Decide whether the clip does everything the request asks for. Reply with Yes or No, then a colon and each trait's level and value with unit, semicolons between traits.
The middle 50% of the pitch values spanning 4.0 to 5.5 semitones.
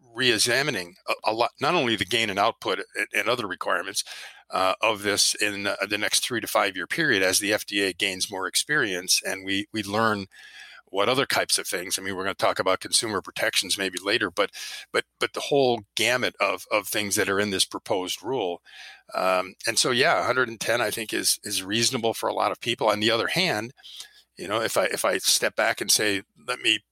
No: average, 2.8 semitones